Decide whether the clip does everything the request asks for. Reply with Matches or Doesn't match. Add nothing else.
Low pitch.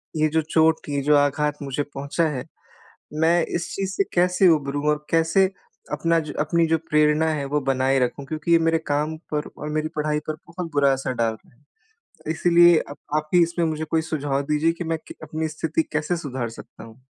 Doesn't match